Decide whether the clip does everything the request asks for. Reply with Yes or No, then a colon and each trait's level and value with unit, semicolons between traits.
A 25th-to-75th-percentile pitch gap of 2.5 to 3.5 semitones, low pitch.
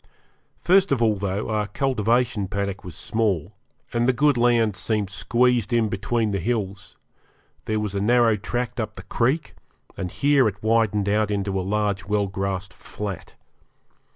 Yes: average, 3.1 semitones; low, 105 Hz